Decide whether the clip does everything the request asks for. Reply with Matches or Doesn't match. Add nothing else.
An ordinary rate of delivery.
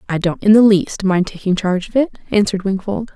Doesn't match